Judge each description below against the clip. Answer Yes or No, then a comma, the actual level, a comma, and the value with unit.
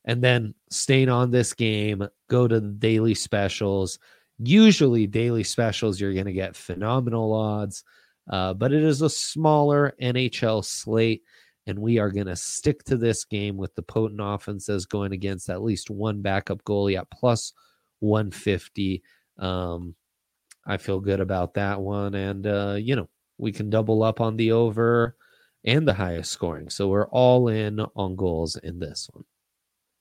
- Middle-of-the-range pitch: No, low, 105 Hz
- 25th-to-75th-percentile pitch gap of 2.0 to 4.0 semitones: Yes, average, 2.9 semitones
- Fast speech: No, average, 165 wpm